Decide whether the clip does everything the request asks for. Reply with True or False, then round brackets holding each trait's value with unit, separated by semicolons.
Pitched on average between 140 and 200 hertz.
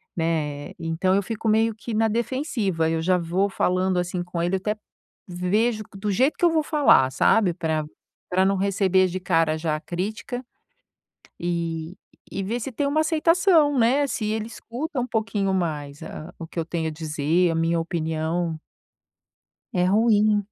True (185 Hz)